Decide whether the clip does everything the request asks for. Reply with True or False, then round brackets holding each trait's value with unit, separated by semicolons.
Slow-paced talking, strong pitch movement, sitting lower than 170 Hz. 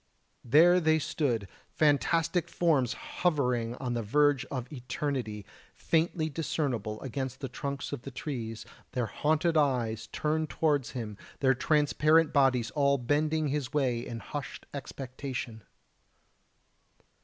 False (120 wpm; 4.0 semitones; 140 Hz)